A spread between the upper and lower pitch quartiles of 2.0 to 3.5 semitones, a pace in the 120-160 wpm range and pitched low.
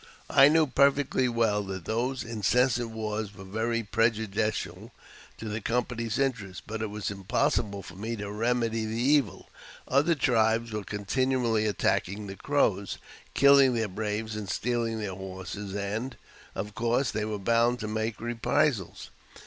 Yes: average, 2.8 semitones; average, 150 wpm; low, 110 Hz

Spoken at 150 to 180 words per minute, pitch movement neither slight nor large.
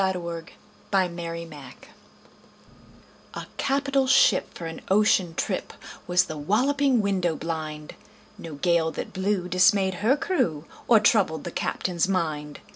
No: slow, 135 wpm; average, 4.1 semitones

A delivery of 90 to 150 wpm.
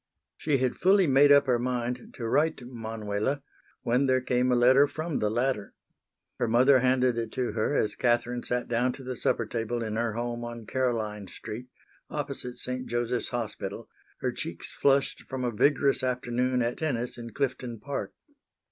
No: average, 175 wpm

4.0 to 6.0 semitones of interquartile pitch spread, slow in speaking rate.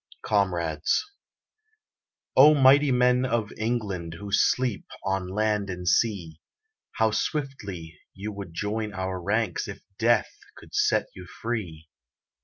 Yes: average, 4.4 semitones; slow, 120 wpm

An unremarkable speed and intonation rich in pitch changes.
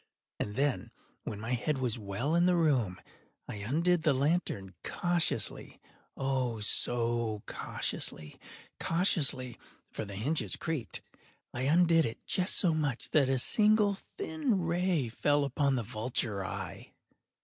No: slow, 125 wpm; wide, 6.5 semitones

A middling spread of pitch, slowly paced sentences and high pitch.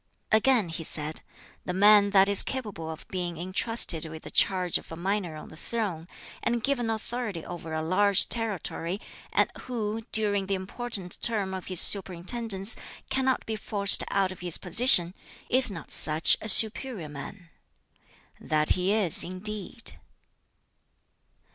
No: average, 4.2 semitones; average, 150 wpm; high, 195 Hz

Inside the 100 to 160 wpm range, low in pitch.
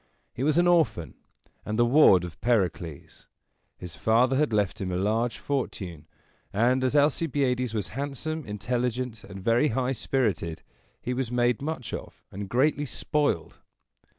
Yes: average, 150 wpm; low, 120 Hz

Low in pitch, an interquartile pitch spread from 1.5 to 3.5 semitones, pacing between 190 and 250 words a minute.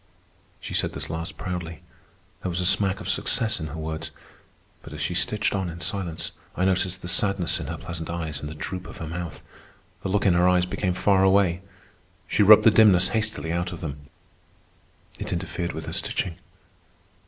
Yes: very low, 90 Hz; average, 2.7 semitones; average, 195 wpm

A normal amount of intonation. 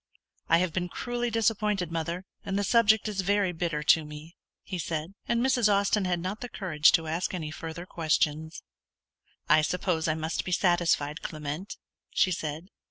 Yes: average, 3.9 semitones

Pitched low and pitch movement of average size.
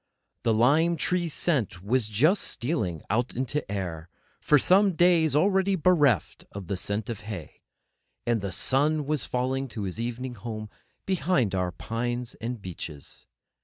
No: low, 120 Hz; wide, 6.9 semitones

